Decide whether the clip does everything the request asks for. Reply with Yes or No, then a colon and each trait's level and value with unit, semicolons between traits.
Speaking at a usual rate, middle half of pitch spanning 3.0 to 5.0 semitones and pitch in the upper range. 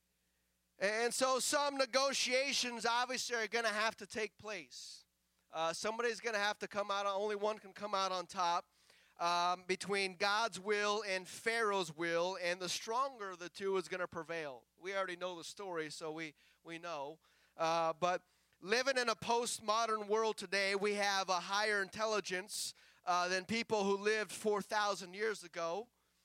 Yes: average, 170 wpm; average, 3.7 semitones; high, 200 Hz